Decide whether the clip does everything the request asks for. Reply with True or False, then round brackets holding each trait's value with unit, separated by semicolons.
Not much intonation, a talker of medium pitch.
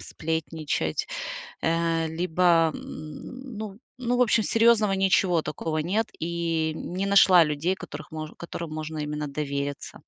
False (3.7 semitones; 165 Hz)